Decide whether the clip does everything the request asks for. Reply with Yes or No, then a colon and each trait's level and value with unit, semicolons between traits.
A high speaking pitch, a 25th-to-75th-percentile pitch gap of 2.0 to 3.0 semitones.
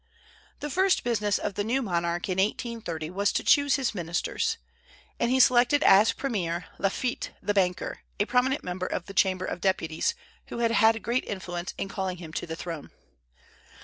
No: high, 200 Hz; average, 5.1 semitones